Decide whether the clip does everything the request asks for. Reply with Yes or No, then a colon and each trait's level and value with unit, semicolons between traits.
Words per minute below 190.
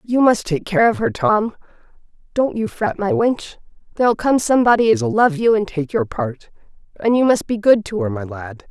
No: average, 195 wpm